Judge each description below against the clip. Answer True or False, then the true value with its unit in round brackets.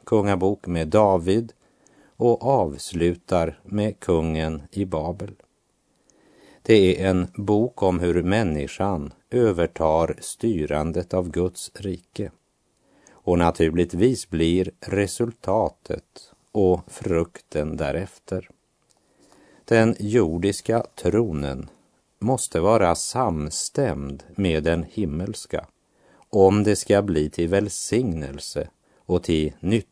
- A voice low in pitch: True (90 Hz)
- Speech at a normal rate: False (90 wpm)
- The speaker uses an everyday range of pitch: True (3.8 semitones)